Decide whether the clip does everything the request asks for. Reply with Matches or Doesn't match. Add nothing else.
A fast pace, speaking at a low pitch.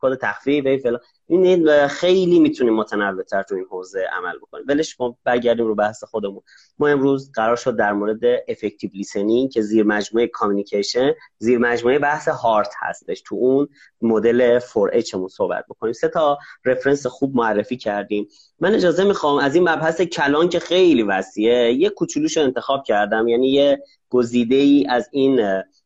Matches